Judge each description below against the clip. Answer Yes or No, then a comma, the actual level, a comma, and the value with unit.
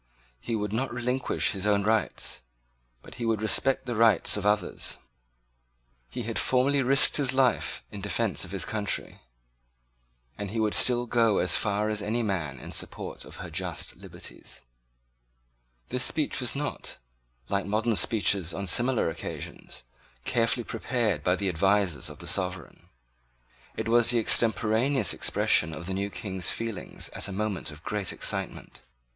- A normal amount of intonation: Yes, average, 3.5 semitones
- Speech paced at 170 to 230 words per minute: No, average, 155 wpm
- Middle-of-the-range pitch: No, low, 110 Hz